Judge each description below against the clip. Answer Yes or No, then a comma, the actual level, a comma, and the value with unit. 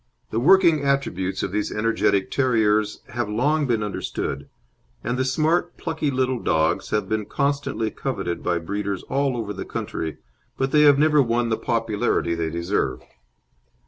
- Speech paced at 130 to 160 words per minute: Yes, average, 155 wpm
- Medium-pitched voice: No, low, 115 Hz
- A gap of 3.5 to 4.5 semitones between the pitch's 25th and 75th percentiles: No, wide, 5.4 semitones